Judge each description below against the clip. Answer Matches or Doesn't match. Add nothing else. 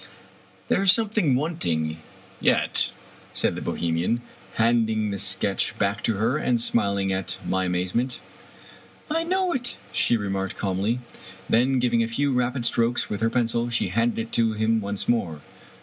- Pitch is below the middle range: Matches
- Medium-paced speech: Matches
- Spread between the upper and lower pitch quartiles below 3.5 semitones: Doesn't match